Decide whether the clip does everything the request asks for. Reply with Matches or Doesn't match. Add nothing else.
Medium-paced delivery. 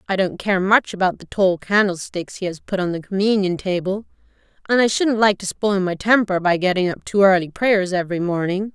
Doesn't match